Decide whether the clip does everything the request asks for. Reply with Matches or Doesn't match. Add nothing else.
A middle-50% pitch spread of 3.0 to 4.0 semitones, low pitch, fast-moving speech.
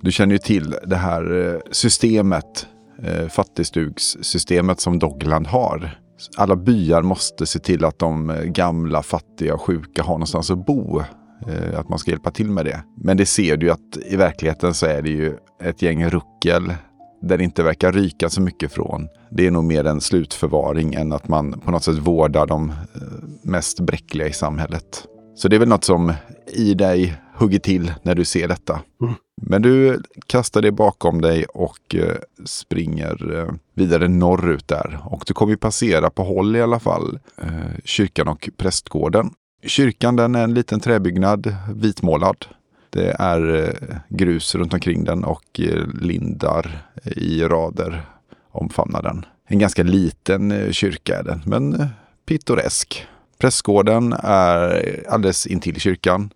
Doesn't match